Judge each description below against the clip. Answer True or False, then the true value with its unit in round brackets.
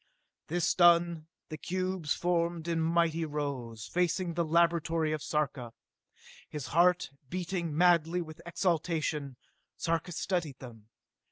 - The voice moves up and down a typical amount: False (2.3 semitones)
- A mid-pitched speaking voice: True (165 Hz)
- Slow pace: True (115 wpm)